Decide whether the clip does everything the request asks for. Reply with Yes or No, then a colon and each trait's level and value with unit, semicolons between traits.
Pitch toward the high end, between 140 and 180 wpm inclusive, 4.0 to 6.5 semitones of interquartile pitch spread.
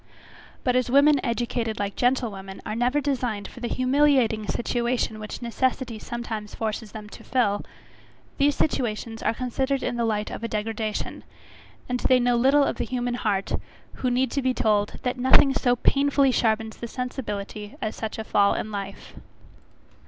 No: high, 240 Hz; average, 165 wpm; average, 3.0 semitones